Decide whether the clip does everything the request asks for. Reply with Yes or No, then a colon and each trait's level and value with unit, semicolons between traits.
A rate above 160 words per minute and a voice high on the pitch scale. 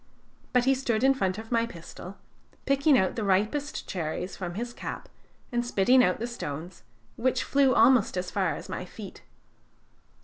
Yes: average, 170 wpm; high, 230 Hz